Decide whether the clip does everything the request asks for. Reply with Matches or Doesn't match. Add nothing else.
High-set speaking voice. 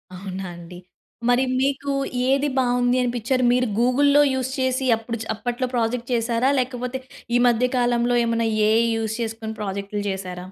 Matches